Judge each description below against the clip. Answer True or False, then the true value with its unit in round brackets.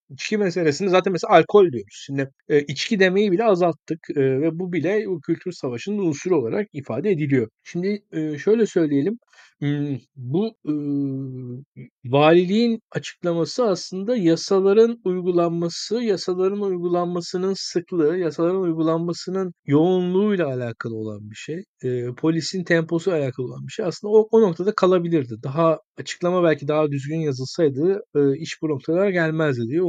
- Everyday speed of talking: True (125 wpm)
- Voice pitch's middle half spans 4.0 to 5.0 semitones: True (4.5 semitones)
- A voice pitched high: False (170 Hz)